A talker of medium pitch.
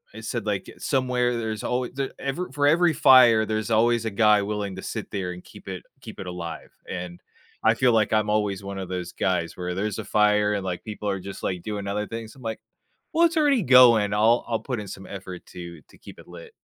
No: low, 105 Hz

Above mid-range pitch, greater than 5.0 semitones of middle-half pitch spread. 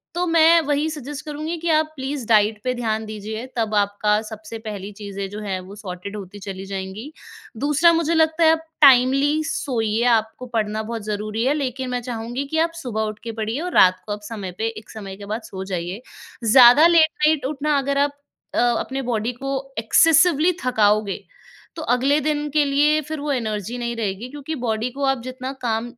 Yes: high, 245 Hz; wide, 5.5 semitones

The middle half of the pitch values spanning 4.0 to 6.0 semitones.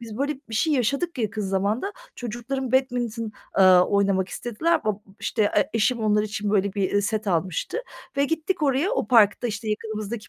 Yes: average, 4.3 semitones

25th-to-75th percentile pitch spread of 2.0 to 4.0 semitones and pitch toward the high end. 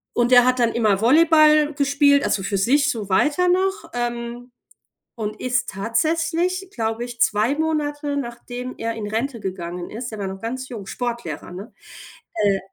No: average, 5.0 semitones; high, 240 Hz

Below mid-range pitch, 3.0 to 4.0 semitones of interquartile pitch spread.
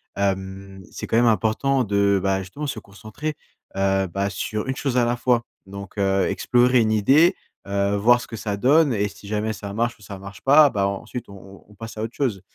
Yes: low, 105 Hz; average, 3.7 semitones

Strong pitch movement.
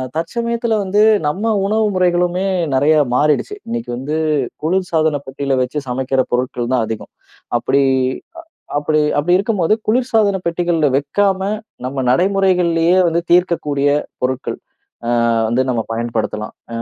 Yes: wide, 6.2 semitones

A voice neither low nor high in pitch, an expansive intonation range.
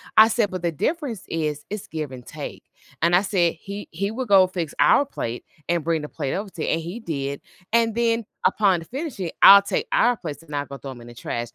Yes: medium, 175 Hz; wide, 6.0 semitones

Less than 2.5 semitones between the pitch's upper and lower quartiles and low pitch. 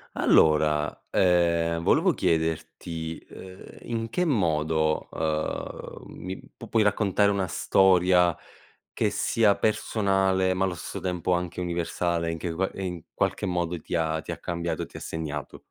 No: average, 2.8 semitones; very low, 90 Hz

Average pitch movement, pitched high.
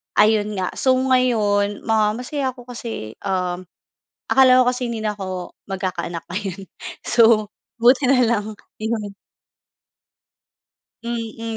Yes: average, 3.6 semitones; high, 220 Hz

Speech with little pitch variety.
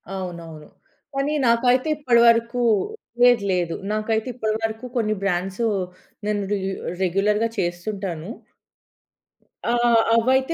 No: average, 3.9 semitones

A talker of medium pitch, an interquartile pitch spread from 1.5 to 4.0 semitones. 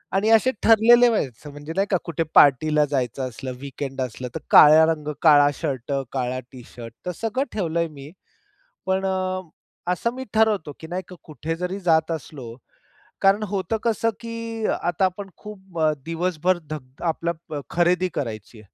No: medium, 165 Hz; average, 5.2 semitones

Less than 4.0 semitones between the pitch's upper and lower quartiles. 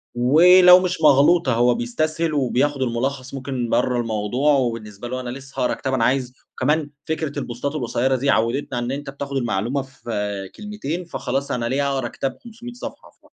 Yes: average, 3.3 semitones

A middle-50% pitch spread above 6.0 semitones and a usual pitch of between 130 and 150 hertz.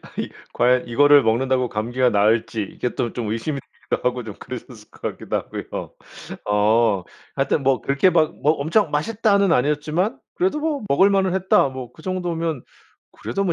Yes: wide, 6.9 semitones; medium, 140 Hz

